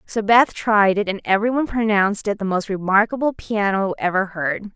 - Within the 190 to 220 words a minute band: No, average, 175 wpm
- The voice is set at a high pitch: Yes, high, 205 Hz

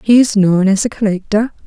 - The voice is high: Yes, high, 210 Hz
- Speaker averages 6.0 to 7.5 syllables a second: No, 5.5 syllables/s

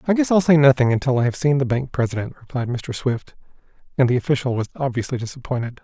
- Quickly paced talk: Yes, fast, 215 wpm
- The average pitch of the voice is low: Yes, low, 130 Hz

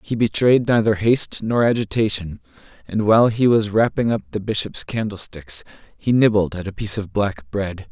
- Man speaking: Yes, male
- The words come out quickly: No, average, 175 wpm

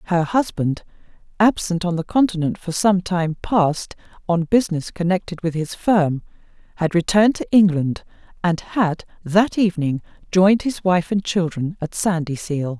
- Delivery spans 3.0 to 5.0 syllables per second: Yes, 4.7 syllables/s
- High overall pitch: No, medium, 180 Hz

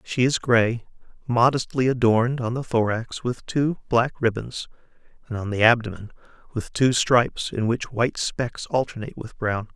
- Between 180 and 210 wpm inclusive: No, average, 160 wpm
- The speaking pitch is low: Yes, low, 120 Hz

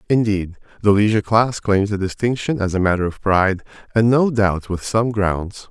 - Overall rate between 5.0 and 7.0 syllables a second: Yes, 5.1 syllables/s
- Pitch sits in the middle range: No, low, 105 Hz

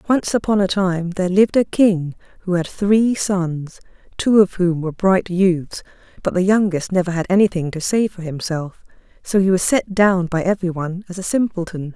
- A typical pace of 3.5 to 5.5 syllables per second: Yes, 5.1 syllables/s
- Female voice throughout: Yes, female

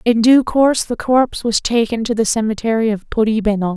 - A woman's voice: Yes, female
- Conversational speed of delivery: Yes, average, 190 wpm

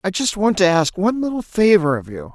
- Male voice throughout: Yes, male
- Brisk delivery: Yes, fast, 255 wpm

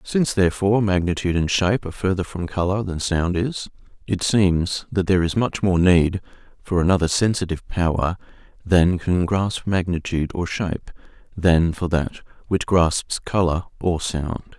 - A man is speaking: Yes, male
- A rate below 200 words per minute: Yes, average, 155 wpm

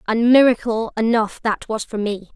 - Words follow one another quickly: No, average, 180 wpm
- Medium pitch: No, high, 225 Hz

